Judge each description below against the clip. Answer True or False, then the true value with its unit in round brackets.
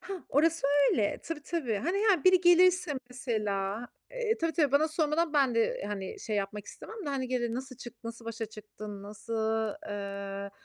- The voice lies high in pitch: True (245 Hz)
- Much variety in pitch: True (7.6 semitones)